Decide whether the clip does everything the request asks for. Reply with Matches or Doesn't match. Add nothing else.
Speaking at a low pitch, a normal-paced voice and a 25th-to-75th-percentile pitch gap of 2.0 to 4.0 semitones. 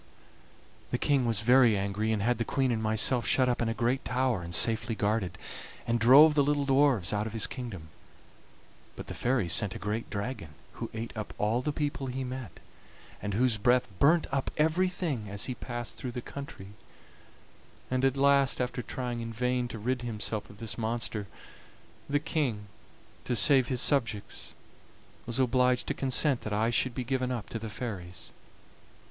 Matches